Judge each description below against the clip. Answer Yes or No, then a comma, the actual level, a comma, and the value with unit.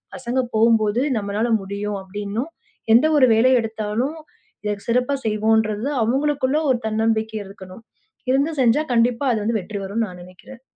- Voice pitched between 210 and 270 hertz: Yes, high, 225 Hz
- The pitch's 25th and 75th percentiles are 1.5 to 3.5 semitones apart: Yes, average, 3.2 semitones